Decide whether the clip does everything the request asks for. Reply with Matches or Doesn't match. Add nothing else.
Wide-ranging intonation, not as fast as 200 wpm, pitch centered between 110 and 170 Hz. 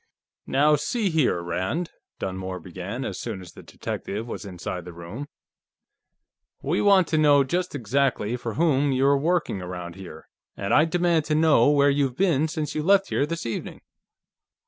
Matches